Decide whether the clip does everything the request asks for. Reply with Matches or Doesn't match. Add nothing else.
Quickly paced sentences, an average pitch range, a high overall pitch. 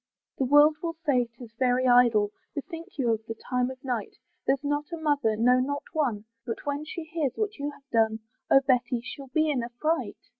Matches